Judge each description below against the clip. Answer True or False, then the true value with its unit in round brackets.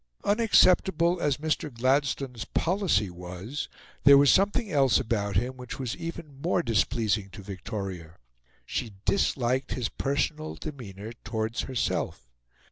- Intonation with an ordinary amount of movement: False (6.4 semitones)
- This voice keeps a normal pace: False (125 wpm)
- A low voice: True (130 Hz)